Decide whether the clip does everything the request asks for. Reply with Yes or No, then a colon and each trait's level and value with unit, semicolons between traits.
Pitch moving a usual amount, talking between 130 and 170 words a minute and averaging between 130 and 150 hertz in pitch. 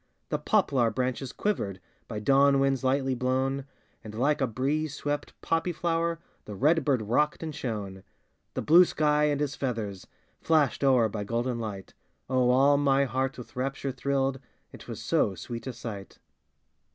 Yes: average, 3.6 semitones; average, 165 wpm; low, 135 Hz